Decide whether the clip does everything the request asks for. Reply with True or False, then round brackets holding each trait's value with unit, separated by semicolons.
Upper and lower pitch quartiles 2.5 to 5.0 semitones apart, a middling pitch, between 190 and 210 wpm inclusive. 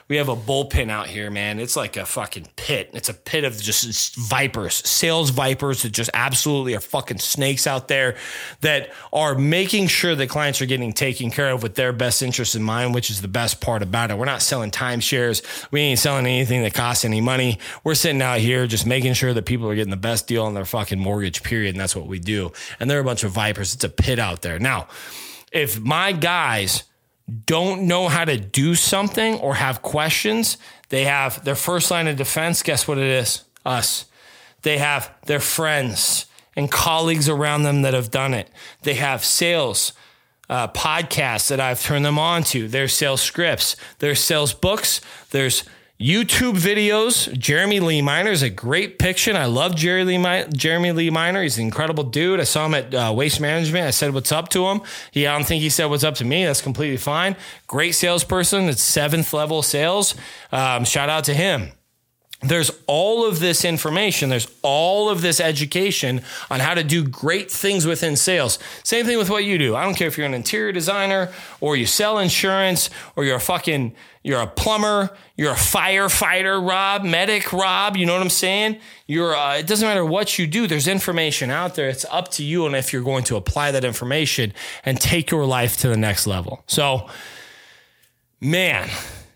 False (5.6 semitones; 145 Hz; 200 wpm)